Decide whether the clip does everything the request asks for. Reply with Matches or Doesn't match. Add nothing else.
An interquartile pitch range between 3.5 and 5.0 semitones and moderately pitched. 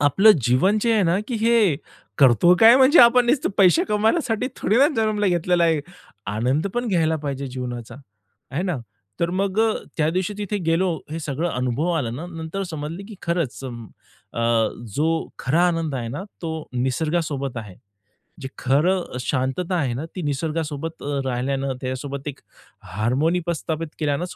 Doesn't match